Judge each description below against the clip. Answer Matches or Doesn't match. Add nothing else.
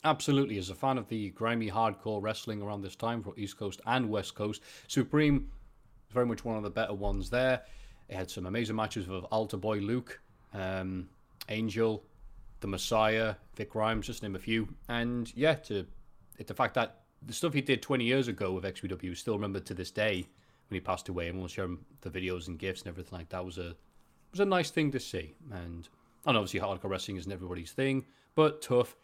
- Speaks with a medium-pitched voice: Doesn't match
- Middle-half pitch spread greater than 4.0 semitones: Matches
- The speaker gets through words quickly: Matches